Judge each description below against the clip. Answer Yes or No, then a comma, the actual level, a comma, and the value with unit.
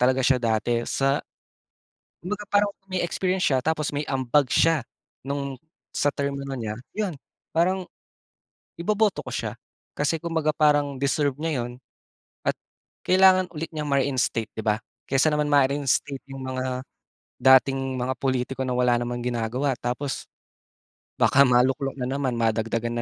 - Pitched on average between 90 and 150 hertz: Yes, low, 135 Hz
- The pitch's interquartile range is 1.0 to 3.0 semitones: No, average, 3.5 semitones